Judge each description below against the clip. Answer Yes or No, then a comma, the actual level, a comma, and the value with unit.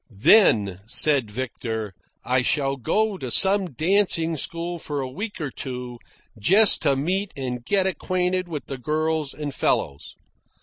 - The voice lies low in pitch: No, medium, 150 Hz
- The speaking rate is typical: Yes, average, 145 wpm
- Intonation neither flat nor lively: No, wide, 6.6 semitones